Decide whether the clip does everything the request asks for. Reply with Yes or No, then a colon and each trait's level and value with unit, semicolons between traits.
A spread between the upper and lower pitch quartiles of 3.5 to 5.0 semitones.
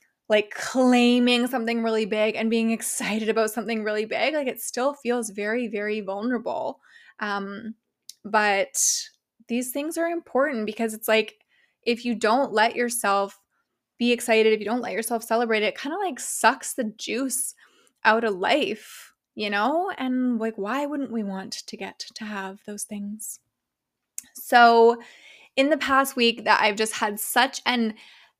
No: average, 2.9 semitones